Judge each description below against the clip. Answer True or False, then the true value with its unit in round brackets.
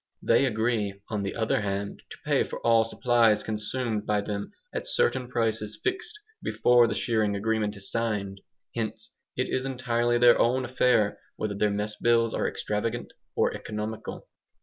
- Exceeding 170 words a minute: False (160 wpm)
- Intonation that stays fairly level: True (2.3 semitones)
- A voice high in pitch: False (110 Hz)